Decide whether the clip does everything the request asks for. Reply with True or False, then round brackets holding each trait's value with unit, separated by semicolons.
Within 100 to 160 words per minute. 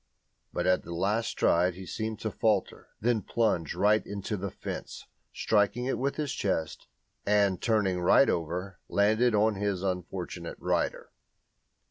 True (145 wpm)